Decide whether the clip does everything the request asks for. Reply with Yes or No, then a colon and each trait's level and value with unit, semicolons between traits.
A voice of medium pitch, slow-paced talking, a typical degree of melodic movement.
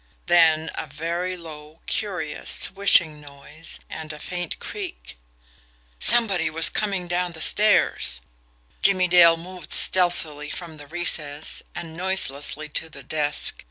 Yes: medium, 165 Hz; slow, 125 wpm; average, 3.0 semitones